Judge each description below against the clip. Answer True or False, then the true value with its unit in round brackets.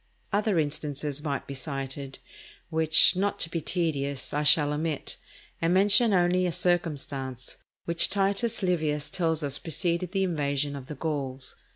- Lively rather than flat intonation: False (3.8 semitones)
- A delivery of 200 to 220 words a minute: False (150 wpm)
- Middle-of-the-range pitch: True (155 Hz)